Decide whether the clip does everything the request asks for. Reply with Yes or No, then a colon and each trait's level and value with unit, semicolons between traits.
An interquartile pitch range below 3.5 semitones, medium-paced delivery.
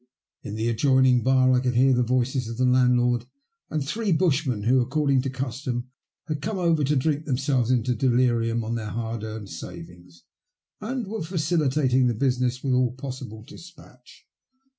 Yes: average, 2.9 semitones; average, 165 wpm